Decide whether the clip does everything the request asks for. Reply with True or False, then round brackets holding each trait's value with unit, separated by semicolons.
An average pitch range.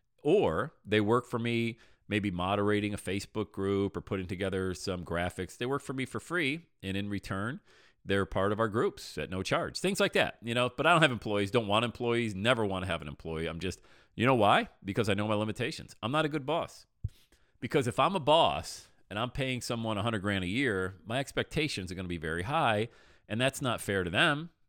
True (4.7 semitones)